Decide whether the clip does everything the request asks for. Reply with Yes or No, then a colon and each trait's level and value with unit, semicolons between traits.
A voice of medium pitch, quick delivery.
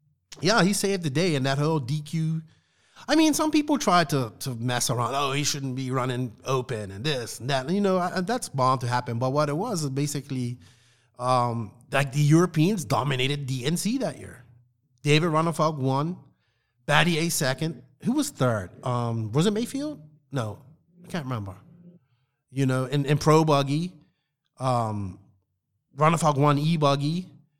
No: medium, 145 Hz; average, 165 wpm